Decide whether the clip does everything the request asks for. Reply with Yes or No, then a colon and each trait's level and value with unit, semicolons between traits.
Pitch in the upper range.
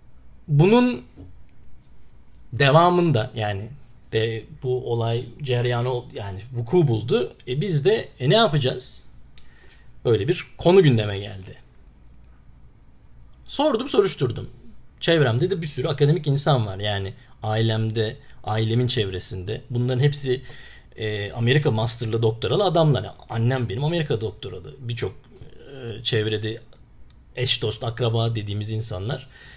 No: low, 120 Hz